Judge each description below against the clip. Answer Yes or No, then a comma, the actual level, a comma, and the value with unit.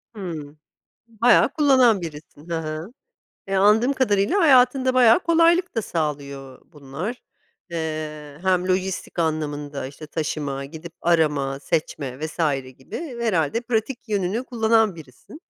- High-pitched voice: No, medium, 175 Hz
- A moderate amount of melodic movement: No, wide, 7.3 semitones